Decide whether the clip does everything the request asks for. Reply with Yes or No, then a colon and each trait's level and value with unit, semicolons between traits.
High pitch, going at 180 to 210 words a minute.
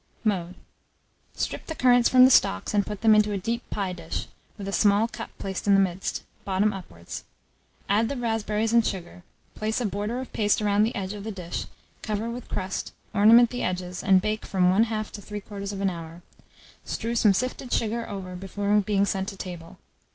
Yes: high, 205 Hz; average, 190 wpm